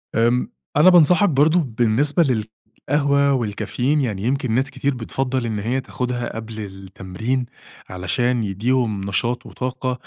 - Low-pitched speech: Yes, low, 125 Hz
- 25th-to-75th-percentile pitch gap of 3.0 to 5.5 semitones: Yes, average, 3.6 semitones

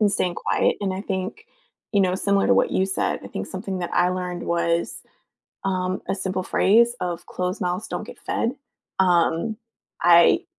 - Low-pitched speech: No, medium, 185 Hz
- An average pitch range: No, narrow, 1.8 semitones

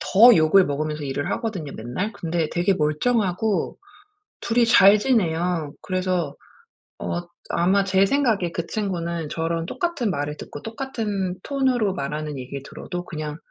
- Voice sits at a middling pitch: Yes, medium, 180 Hz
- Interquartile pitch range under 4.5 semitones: No, wide, 5.4 semitones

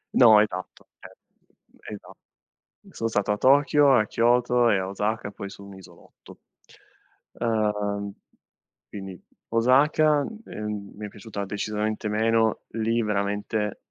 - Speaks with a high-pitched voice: No, low, 105 Hz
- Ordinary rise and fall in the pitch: No, narrow, 2.2 semitones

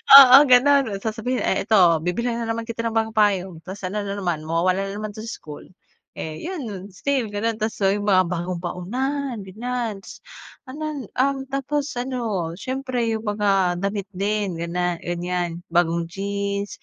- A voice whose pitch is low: No, high, 205 Hz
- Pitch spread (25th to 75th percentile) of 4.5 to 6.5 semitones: Yes, average, 5.1 semitones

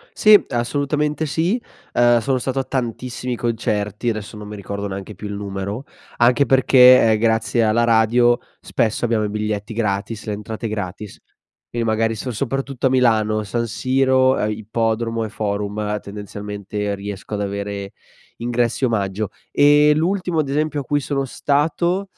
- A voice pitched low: Yes, low, 115 Hz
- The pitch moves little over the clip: No, average, 4.0 semitones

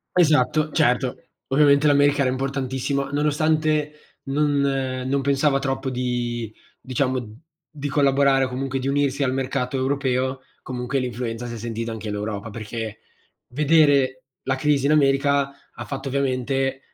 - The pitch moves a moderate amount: No, narrow, 2.0 semitones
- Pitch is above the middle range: No, low, 135 Hz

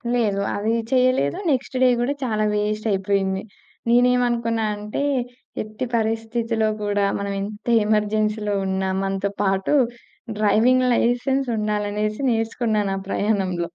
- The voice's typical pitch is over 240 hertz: No, high, 215 Hz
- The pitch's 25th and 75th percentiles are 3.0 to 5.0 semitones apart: No, narrow, 2.4 semitones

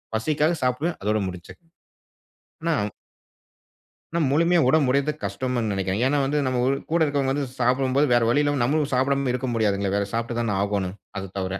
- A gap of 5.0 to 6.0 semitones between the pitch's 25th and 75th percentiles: Yes, wide, 5.4 semitones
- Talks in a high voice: No, low, 125 Hz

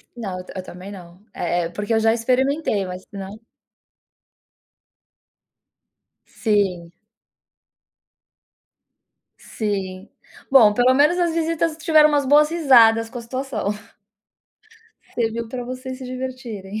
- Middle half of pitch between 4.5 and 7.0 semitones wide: Yes, average, 5.1 semitones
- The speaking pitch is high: Yes, high, 230 Hz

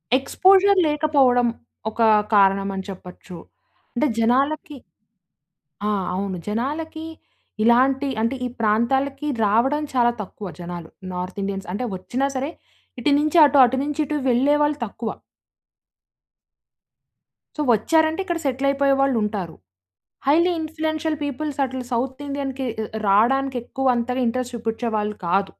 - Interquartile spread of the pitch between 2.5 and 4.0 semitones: No, average, 5.0 semitones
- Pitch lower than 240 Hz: No, very high, 260 Hz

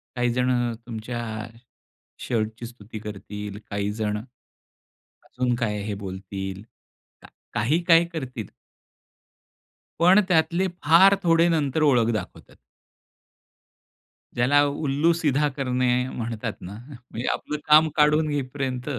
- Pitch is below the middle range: Yes, low, 125 Hz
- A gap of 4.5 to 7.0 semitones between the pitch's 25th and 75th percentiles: Yes, wide, 5.6 semitones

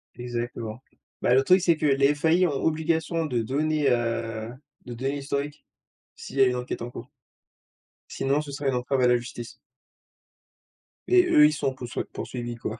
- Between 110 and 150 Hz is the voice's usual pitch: Yes, low, 135 Hz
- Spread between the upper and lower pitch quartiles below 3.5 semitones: No, average, 3.8 semitones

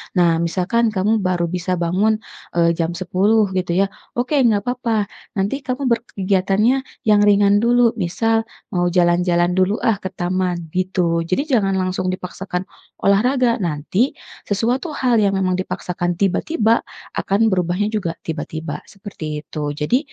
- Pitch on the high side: Yes, high, 195 Hz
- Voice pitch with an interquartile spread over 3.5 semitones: Yes, average, 4.0 semitones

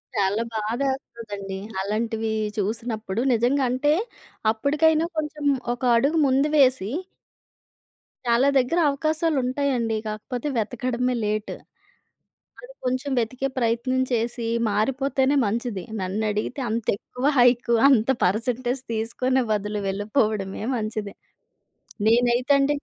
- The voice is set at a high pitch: Yes, high, 240 Hz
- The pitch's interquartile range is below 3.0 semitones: No, average, 3.7 semitones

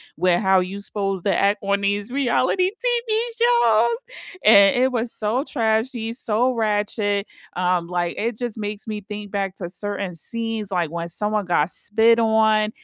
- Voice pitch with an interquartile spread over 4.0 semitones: No, average, 2.8 semitones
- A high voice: Yes, high, 210 Hz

